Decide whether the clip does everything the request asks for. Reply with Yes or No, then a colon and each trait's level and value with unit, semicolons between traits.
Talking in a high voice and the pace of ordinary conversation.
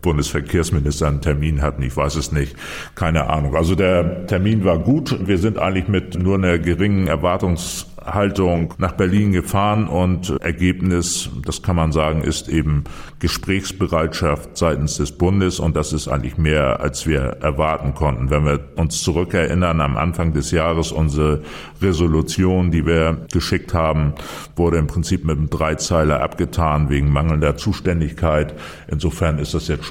No: very low, 80 Hz; average, 155 wpm